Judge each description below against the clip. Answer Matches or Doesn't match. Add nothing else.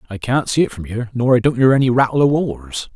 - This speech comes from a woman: Doesn't match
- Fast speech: Matches